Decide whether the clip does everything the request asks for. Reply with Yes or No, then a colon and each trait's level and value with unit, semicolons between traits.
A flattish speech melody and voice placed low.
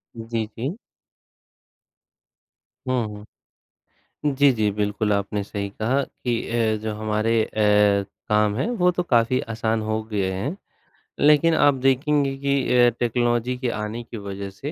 No: average, 3.5 semitones; low, 115 Hz